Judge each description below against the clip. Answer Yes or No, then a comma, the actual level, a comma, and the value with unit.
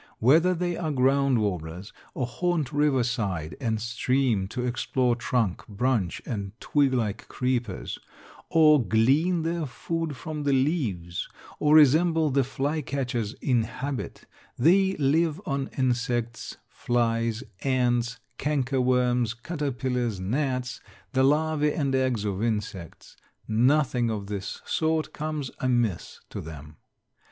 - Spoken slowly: Yes, slow, 125 wpm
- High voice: No, low, 125 Hz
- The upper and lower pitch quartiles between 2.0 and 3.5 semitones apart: No, average, 4.3 semitones